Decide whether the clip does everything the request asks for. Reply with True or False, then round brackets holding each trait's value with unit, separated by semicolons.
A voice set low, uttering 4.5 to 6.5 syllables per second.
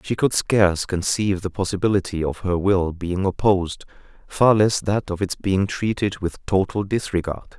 True (95 Hz; 5.0 syllables/s)